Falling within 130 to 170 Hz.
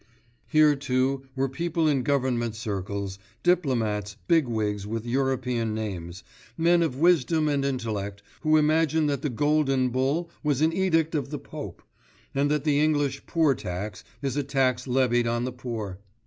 Yes: low, 135 Hz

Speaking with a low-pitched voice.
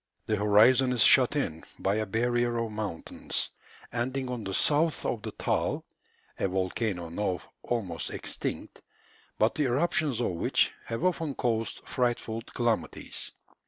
Yes: low, 115 Hz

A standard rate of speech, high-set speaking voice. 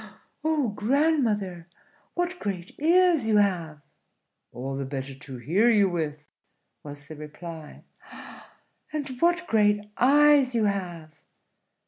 No: slow, 115 wpm; high, 205 Hz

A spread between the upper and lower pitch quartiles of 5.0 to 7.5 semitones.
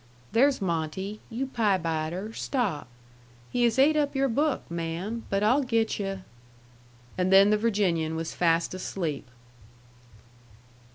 Yes: wide, 5.6 semitones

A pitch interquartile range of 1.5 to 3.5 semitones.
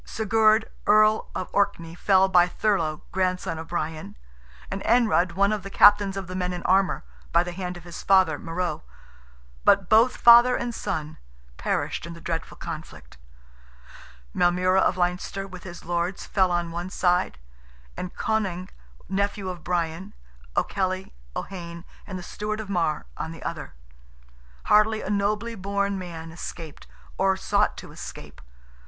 Yes: average, 2.7 semitones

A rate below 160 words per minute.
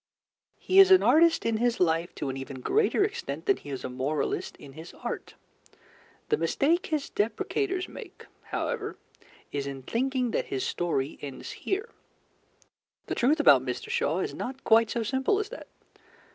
No: average, 170 wpm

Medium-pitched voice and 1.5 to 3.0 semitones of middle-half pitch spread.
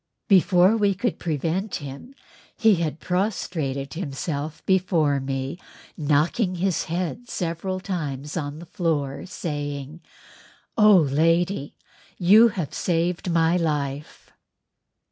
No: medium, 165 Hz; average, 4.3 semitones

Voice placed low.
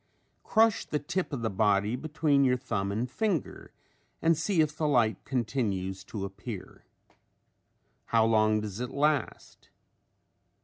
Yes: low, 125 Hz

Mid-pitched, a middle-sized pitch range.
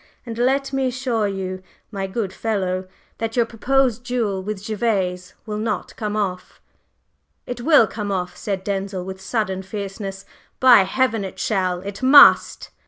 No: high, 210 Hz; average, 3.7 semitones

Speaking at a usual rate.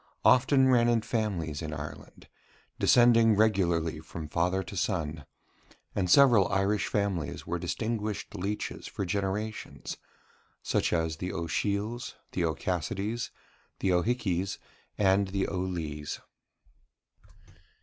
No: slow, 110 wpm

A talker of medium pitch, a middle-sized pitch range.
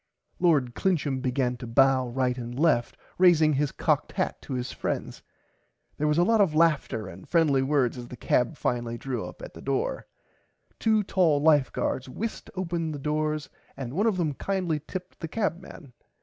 Yes: medium, 150 Hz; average, 5.0 semitones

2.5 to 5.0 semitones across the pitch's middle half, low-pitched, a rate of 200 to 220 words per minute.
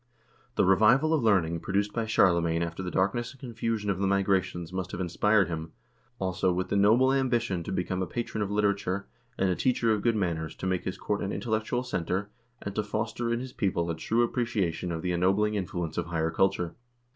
Yes: average, 3.7 semitones; low, 100 Hz; fast, 205 wpm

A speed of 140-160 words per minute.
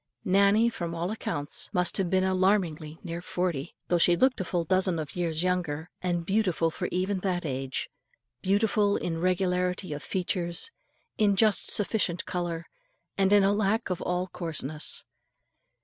Yes: average, 155 wpm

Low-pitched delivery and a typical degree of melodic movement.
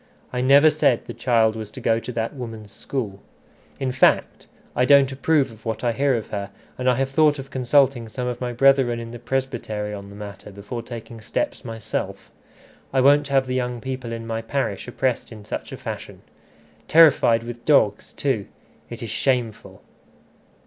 Yes: low, 120 Hz; average, 3.0 semitones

